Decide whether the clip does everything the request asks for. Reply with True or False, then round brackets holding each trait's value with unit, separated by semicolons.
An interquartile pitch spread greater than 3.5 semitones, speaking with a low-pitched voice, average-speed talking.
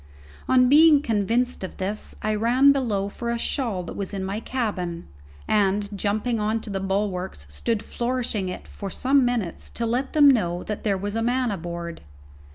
False (4.2 semitones; 215 Hz; 180 wpm)